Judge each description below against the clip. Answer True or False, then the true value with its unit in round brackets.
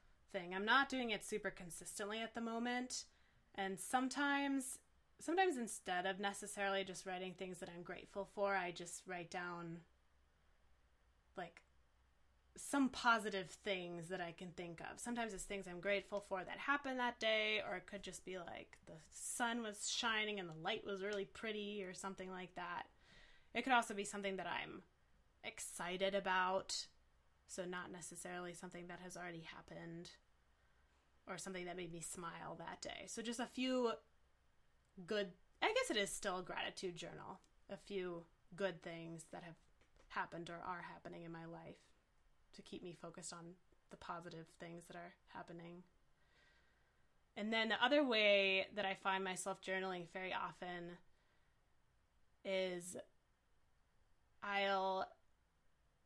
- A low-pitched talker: False (185 Hz)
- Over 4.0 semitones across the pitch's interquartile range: False (3.0 semitones)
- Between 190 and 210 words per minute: False (150 wpm)